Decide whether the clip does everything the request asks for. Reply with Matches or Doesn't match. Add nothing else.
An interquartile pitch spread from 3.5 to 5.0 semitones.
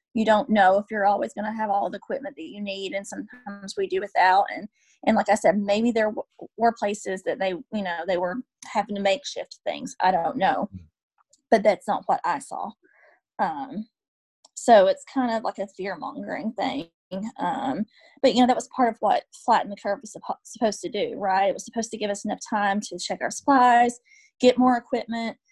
Matches